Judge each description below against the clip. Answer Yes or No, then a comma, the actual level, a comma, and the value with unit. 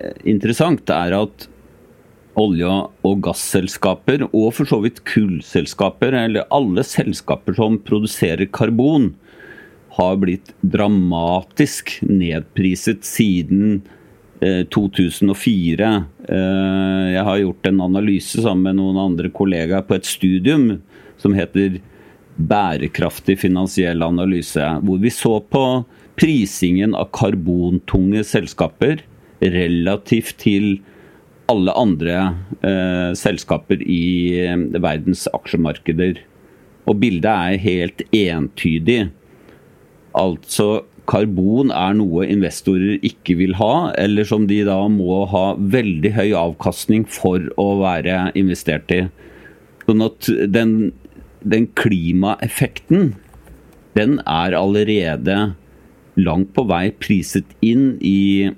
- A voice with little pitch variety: Yes, narrow, 2.2 semitones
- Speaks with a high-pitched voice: No, very low, 95 Hz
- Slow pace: Yes, slow, 100 wpm